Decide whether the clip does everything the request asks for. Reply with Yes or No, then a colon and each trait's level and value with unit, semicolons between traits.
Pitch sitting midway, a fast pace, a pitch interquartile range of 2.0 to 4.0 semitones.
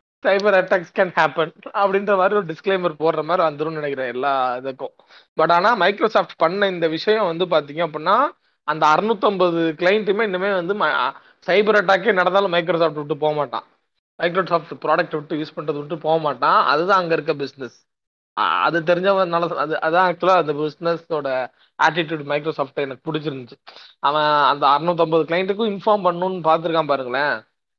Yes: medium, 165 Hz; fast, 145 wpm; average, 3.6 semitones